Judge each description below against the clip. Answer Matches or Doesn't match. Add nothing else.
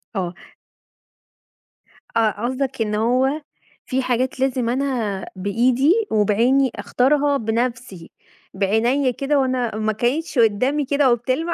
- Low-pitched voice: Doesn't match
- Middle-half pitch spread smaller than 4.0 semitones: Matches